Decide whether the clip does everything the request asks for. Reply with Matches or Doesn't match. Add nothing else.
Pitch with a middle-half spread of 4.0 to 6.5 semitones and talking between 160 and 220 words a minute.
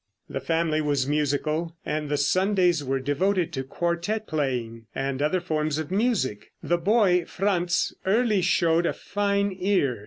Doesn't match